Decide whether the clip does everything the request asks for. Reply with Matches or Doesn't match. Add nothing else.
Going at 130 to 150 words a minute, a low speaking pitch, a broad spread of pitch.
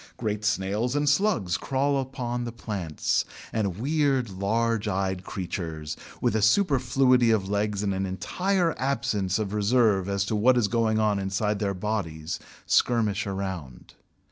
Doesn't match